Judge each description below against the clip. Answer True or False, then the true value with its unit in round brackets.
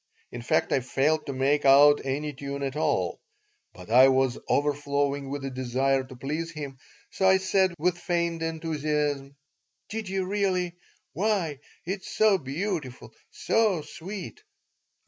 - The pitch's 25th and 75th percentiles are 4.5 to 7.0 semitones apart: True (4.8 semitones)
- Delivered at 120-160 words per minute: True (145 wpm)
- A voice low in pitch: False (150 Hz)